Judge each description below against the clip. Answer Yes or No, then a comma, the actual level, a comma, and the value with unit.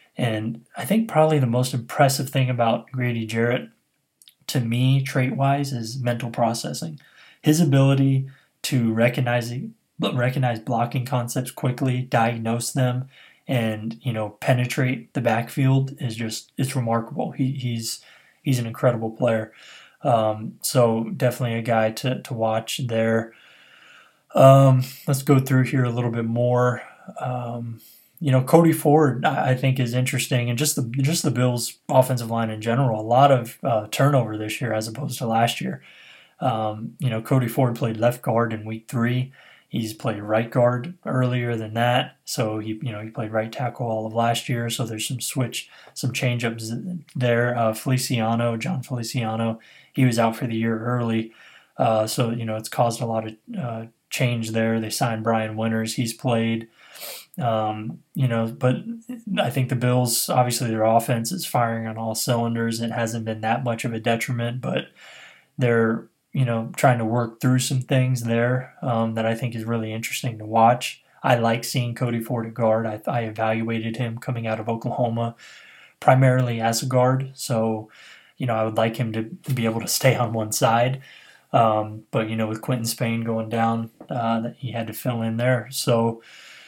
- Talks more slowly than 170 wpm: No, average, 175 wpm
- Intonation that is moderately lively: No, narrow, 2.3 semitones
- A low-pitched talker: Yes, low, 120 Hz